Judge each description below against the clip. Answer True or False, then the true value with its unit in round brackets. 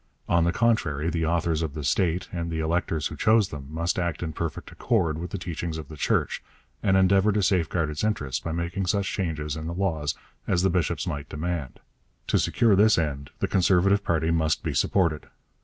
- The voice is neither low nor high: False (85 Hz)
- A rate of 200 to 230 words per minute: True (205 wpm)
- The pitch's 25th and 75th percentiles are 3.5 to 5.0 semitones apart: False (3.1 semitones)